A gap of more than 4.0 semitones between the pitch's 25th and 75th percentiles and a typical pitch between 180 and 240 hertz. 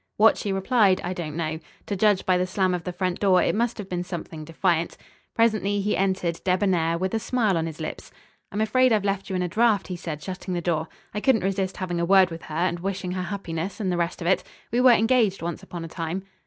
No: average, 2.9 semitones; medium, 185 Hz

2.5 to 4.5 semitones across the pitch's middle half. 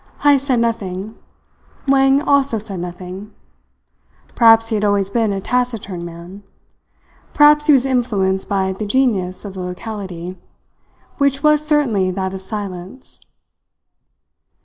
No: wide, 5.6 semitones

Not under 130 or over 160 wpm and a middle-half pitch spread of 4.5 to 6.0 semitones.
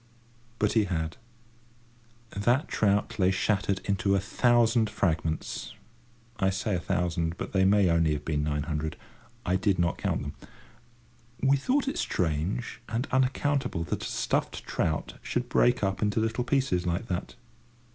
Yes: average, 150 wpm; wide, 5.5 semitones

